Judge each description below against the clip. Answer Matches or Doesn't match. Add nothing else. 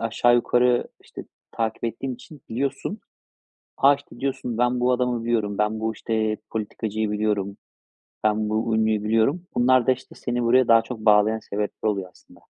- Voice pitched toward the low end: Matches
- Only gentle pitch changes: Matches